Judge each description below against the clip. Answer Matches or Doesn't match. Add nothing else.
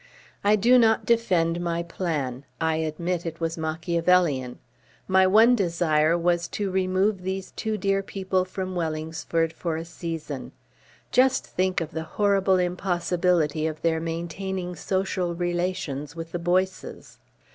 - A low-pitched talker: Doesn't match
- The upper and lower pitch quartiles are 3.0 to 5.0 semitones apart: Doesn't match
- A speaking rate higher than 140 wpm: Doesn't match